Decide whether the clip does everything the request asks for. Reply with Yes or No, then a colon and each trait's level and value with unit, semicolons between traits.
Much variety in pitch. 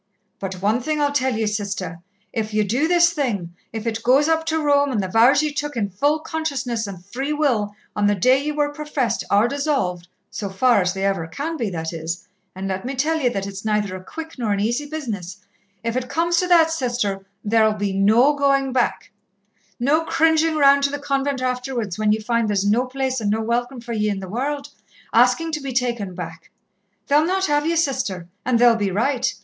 Yes: wide, 5.9 semitones